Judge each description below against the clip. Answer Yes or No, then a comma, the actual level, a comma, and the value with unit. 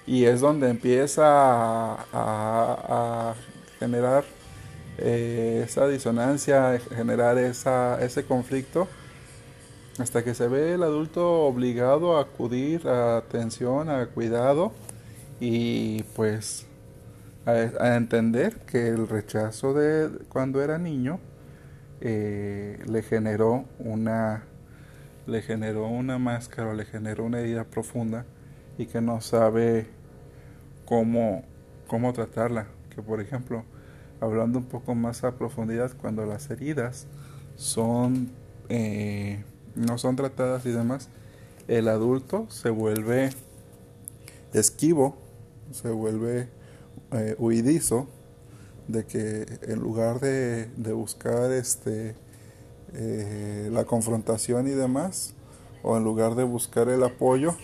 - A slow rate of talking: Yes, slow, 115 wpm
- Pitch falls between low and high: No, low, 120 Hz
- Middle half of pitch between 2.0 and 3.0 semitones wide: Yes, narrow, 2.4 semitones